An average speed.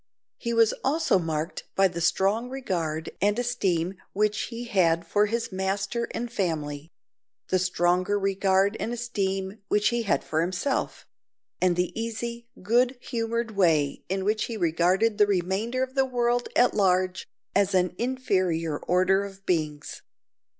Yes: average, 150 wpm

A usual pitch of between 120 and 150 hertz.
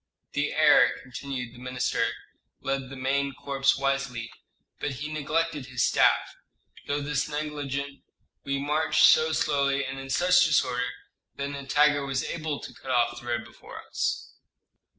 Yes: medium, 140 Hz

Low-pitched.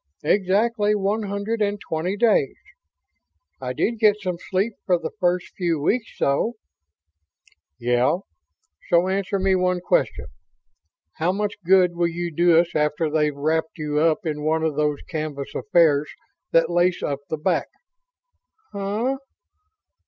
No: medium, 175 Hz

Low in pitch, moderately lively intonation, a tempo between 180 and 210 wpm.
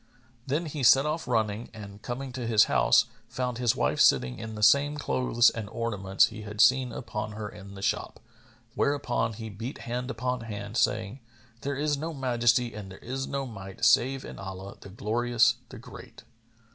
Yes: low, 115 Hz; average, 3.4 semitones; average, 185 wpm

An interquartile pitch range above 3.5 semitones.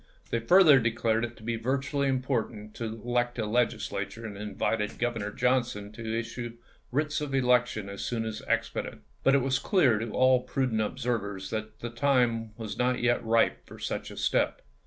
No: narrow, 2.5 semitones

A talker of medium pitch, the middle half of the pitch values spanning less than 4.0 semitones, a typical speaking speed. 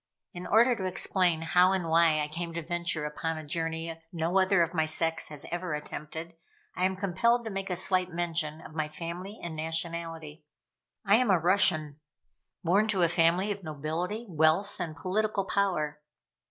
Yes: medium, 170 Hz; average, 2.9 semitones; average, 180 wpm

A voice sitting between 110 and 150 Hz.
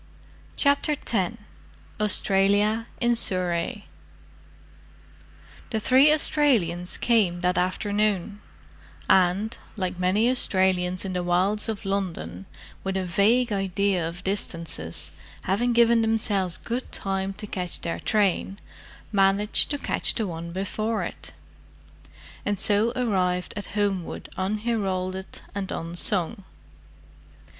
No: high, 195 Hz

